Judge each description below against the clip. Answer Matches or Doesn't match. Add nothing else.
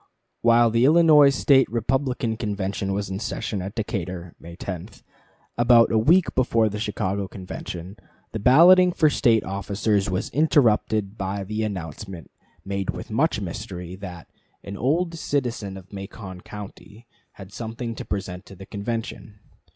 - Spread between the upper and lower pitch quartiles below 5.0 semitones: Matches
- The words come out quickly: Doesn't match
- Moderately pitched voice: Doesn't match